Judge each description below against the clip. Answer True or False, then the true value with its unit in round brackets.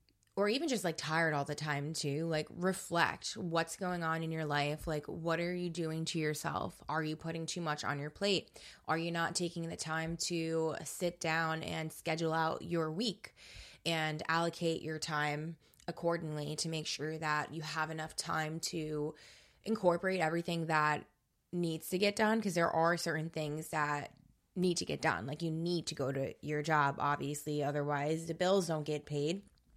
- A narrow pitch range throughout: True (1.9 semitones)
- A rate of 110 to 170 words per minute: False (185 wpm)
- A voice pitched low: False (160 Hz)